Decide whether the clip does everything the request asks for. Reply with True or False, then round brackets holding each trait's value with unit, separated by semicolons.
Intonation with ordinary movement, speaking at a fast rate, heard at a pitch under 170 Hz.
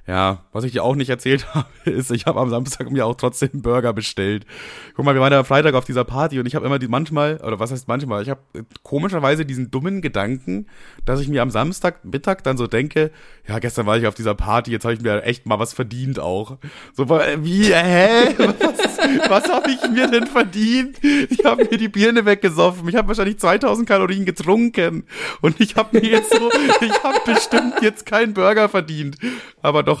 False (8.5 semitones; 210 wpm; 140 Hz)